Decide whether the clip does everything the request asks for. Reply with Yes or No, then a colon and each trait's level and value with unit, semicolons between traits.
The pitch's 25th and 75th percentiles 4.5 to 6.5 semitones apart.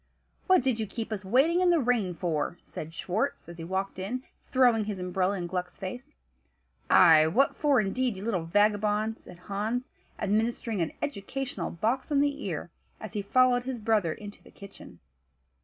Yes: average, 5.1 semitones